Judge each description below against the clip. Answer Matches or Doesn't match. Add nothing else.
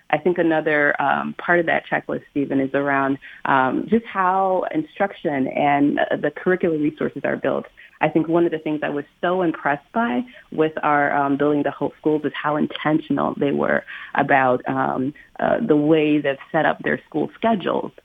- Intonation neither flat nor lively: Matches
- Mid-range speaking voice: Matches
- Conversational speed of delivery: Matches